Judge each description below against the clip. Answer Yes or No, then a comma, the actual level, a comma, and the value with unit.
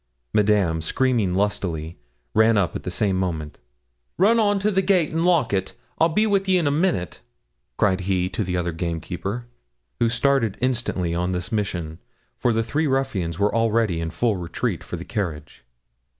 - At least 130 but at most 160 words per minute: No, average, 180 wpm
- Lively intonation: Yes, wide, 7.1 semitones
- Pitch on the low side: Yes, low, 105 Hz